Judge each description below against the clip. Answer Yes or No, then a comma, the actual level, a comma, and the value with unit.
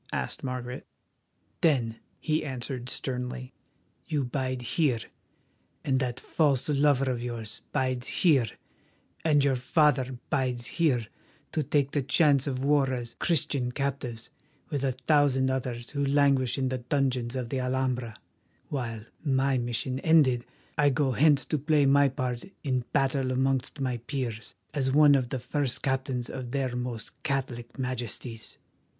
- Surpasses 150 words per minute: No, average, 145 wpm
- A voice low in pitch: Yes, low, 130 Hz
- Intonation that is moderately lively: No, narrow, 2.2 semitones